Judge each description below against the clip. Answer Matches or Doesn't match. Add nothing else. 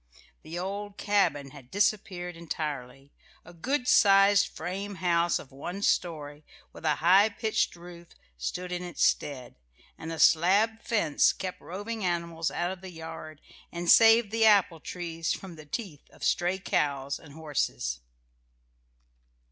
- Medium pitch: Matches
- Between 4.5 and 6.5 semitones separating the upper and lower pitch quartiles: Doesn't match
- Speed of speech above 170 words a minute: Doesn't match